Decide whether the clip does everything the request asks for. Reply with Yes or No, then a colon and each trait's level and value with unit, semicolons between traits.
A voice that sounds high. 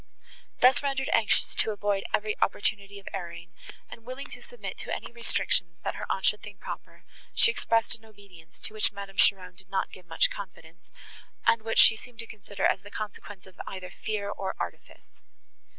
Yes: high, 205 Hz